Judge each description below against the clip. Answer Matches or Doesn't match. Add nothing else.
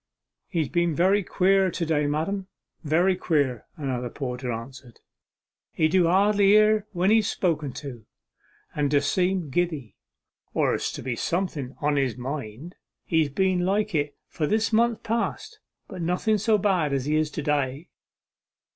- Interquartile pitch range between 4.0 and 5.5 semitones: Matches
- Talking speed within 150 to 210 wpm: Matches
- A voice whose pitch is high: Doesn't match